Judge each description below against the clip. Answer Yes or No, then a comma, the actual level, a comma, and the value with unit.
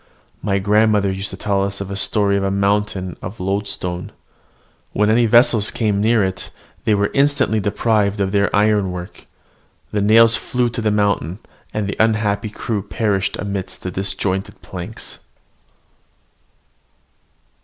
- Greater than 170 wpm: No, average, 140 wpm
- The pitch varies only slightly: Yes, narrow, 1.8 semitones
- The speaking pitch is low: Yes, low, 100 Hz